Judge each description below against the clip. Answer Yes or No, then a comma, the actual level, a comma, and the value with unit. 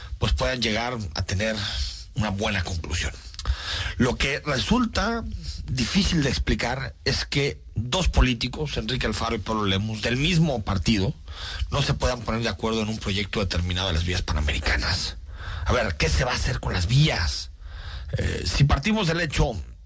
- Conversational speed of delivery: Yes, average, 165 wpm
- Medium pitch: No, low, 100 Hz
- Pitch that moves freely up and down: Yes, wide, 6.2 semitones